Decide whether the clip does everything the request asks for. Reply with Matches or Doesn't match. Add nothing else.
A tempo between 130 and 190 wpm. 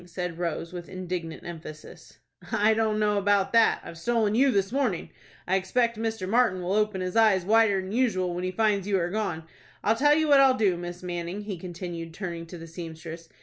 Doesn't match